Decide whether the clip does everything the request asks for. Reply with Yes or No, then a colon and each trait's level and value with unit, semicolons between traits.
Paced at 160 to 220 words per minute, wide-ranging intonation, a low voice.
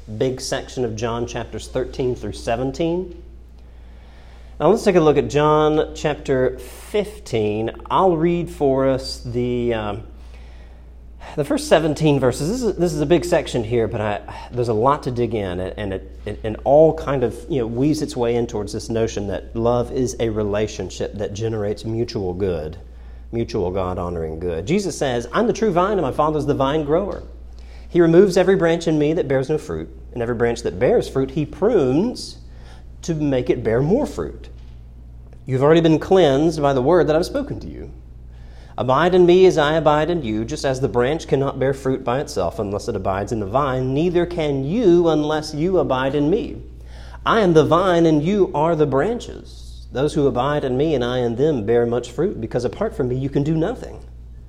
Yes: average, 200 wpm; wide, 7.5 semitones; low, 125 Hz